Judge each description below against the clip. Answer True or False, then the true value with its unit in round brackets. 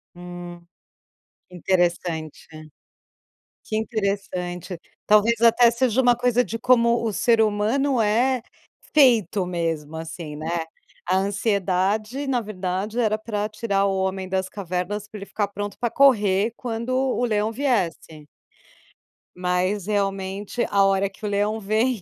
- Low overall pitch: False (205 Hz)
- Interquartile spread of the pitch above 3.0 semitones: True (3.9 semitones)